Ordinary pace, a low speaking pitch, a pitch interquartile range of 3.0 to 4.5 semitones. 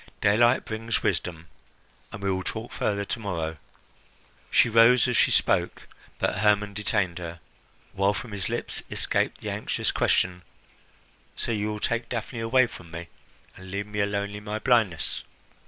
Yes: average, 160 wpm; low, 105 Hz; average, 3.3 semitones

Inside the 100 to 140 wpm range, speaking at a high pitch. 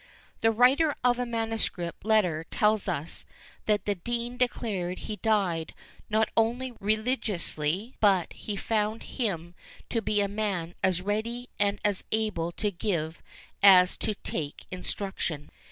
Yes: slow, 135 wpm; high, 210 Hz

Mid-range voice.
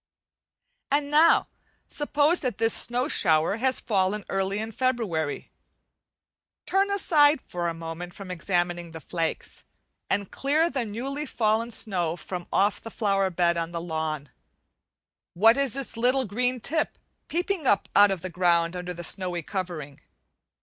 No: high, 200 Hz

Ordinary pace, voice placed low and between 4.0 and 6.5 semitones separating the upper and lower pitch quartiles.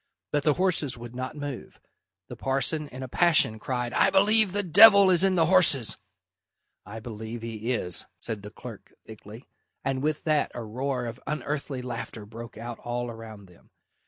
Yes: average, 175 wpm; low, 130 Hz; average, 5.2 semitones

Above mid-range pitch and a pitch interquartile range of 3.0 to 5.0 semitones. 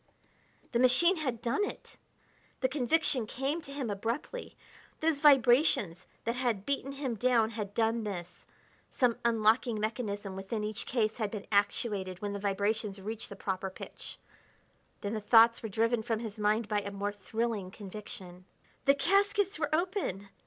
Yes: high, 225 Hz; average, 4.0 semitones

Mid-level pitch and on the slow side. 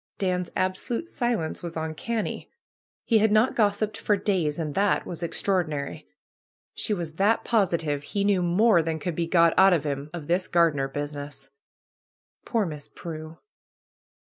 No: medium, 175 Hz; average, 155 wpm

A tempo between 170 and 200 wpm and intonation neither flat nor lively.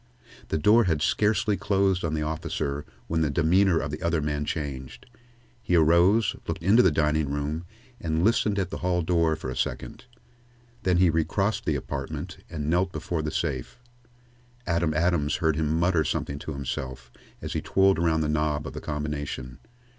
Yes: average, 175 wpm; average, 3.3 semitones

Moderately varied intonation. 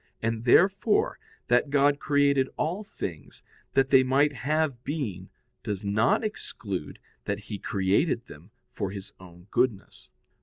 No: wide, 6.3 semitones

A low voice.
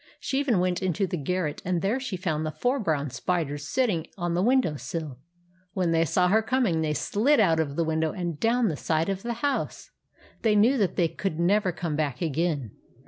No: medium, 175 Hz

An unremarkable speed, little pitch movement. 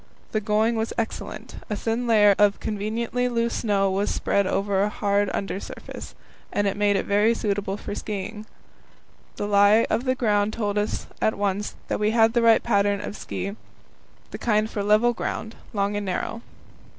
Yes: average, 175 wpm; narrow, 1.8 semitones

